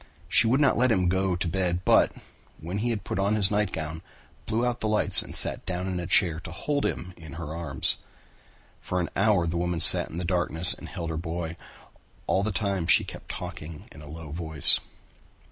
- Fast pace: Yes, fast, 215 wpm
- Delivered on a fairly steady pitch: No, average, 3.5 semitones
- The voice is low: Yes, very low, 90 Hz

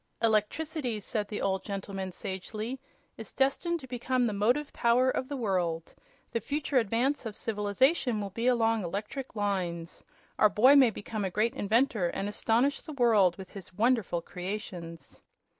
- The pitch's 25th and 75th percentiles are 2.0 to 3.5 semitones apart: No, average, 4.5 semitones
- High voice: Yes, high, 220 Hz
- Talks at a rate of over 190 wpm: No, average, 160 wpm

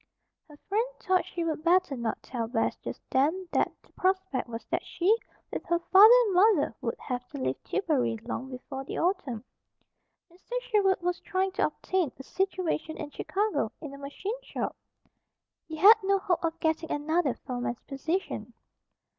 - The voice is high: Yes, very high, 335 Hz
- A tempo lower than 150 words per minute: No, average, 170 wpm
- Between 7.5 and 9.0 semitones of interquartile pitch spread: No, wide, 5.9 semitones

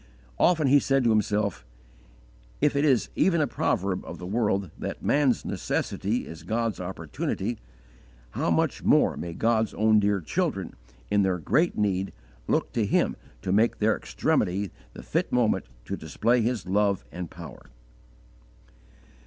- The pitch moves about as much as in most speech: Yes, average, 4.3 semitones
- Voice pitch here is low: Yes, low, 105 Hz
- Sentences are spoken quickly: No, average, 150 wpm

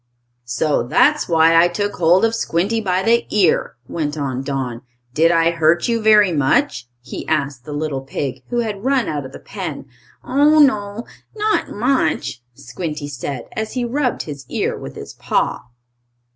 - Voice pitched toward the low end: No, medium, 170 Hz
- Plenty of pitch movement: Yes, wide, 7.7 semitones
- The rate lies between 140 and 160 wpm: No, average, 170 wpm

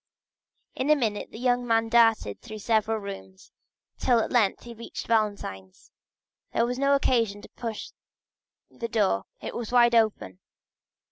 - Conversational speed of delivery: Yes, average, 150 wpm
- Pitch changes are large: No, narrow, 2.6 semitones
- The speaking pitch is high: Yes, high, 225 Hz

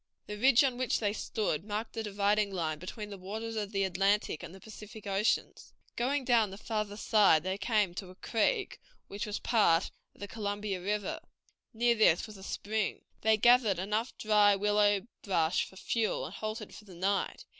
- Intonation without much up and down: Yes, narrow, 2.1 semitones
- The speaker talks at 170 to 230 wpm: Yes, average, 190 wpm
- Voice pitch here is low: No, high, 210 Hz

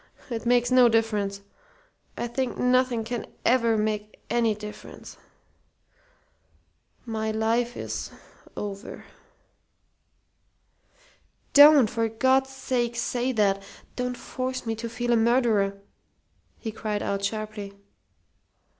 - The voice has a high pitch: Yes, high, 230 Hz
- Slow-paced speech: Yes, slow, 105 wpm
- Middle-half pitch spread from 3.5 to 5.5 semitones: No, narrow, 2.5 semitones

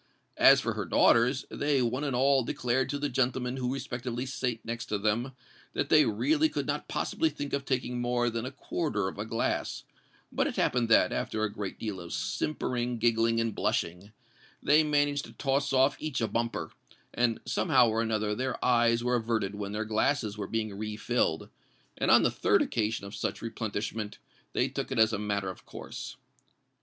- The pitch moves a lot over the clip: No, average, 3.2 semitones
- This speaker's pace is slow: No, average, 190 wpm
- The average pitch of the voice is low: Yes, low, 120 Hz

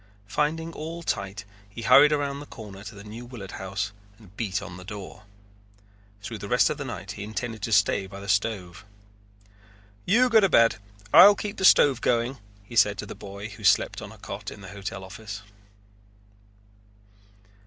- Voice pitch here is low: Yes, low, 105 Hz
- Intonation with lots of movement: Yes, wide, 5.9 semitones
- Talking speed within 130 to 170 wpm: No, average, 185 wpm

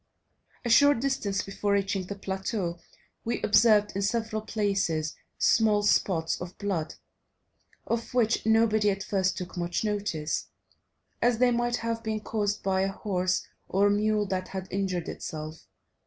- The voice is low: No, high, 205 Hz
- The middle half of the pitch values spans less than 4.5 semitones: Yes, average, 2.7 semitones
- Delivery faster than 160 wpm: No, average, 145 wpm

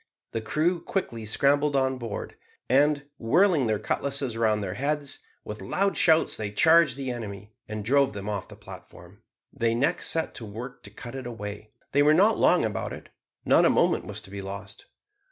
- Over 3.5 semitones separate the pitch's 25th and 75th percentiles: Yes, average, 5.3 semitones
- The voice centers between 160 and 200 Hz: No, low, 120 Hz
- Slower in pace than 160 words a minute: No, average, 190 wpm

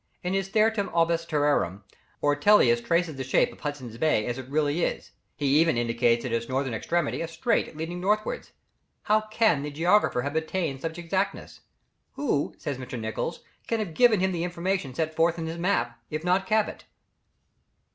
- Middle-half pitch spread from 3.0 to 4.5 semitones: No, wide, 5.6 semitones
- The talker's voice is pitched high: No, medium, 160 Hz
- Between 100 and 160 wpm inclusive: No, average, 180 wpm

